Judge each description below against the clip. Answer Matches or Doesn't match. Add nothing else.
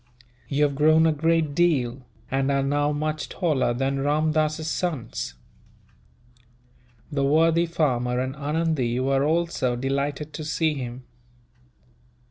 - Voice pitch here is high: Doesn't match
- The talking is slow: Matches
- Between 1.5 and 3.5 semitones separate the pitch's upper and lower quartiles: Matches